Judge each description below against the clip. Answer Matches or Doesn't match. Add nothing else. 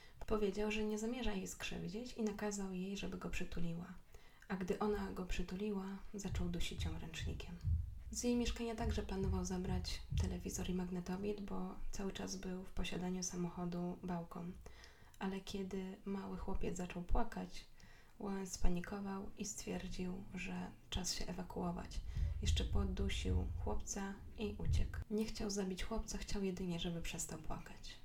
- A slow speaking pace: Doesn't match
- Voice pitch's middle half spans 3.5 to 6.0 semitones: Doesn't match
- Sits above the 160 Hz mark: Matches